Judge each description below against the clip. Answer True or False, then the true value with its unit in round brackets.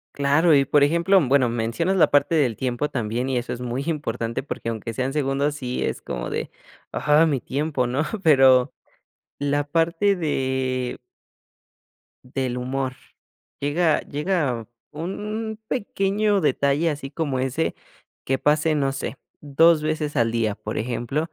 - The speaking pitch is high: False (140 Hz)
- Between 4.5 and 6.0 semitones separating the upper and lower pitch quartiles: False (3.8 semitones)